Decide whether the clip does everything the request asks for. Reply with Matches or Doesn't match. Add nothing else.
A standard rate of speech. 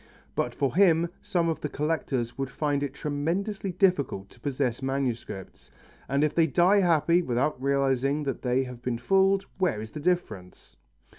Matches